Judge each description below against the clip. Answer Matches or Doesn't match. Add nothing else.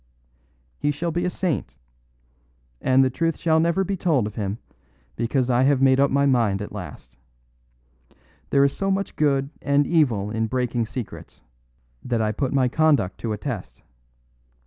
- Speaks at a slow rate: Doesn't match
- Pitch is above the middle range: Doesn't match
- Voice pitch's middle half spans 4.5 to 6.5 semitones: Matches